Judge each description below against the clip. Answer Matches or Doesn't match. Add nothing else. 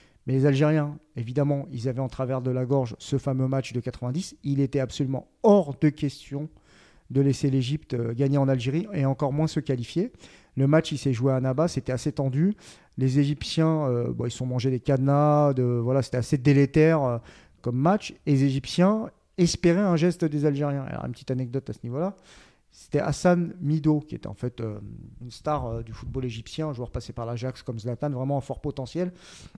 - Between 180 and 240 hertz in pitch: Doesn't match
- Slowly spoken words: Doesn't match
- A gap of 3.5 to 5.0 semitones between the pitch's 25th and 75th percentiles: Doesn't match